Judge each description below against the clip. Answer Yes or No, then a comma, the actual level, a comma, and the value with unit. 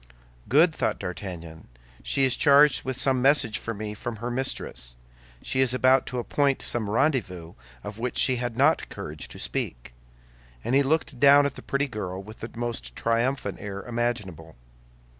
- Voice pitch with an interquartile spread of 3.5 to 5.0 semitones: Yes, average, 4.7 semitones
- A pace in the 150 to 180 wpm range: Yes, average, 170 wpm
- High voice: No, low, 120 Hz